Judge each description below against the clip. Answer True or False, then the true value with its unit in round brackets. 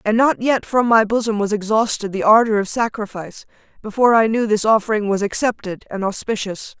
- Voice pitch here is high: True (215 Hz)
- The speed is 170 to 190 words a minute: True (185 wpm)